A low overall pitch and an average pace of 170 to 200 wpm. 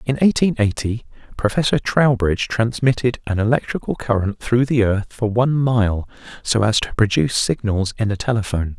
No: low, 115 Hz; average, 155 wpm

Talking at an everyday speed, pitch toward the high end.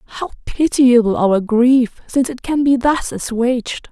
Yes: average, 155 wpm; very high, 250 Hz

